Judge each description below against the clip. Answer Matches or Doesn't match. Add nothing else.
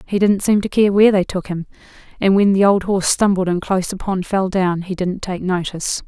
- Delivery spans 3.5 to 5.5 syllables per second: Doesn't match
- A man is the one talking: Doesn't match